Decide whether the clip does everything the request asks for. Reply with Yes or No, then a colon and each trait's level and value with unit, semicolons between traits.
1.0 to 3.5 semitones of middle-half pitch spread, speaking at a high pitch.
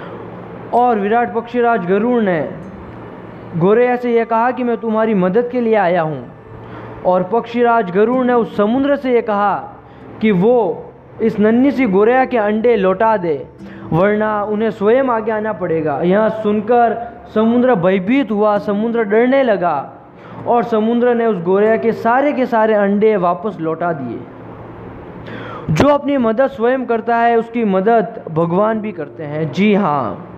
Yes: average, 3.0 semitones; high, 220 Hz